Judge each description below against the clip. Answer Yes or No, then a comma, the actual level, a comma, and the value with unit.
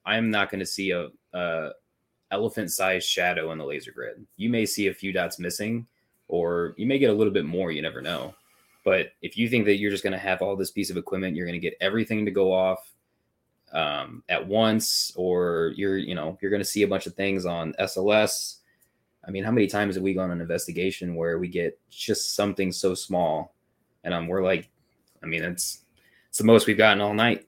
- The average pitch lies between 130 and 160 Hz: No, very low, 95 Hz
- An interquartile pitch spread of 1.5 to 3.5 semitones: Yes, average, 2.8 semitones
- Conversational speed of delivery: No, fast, 225 wpm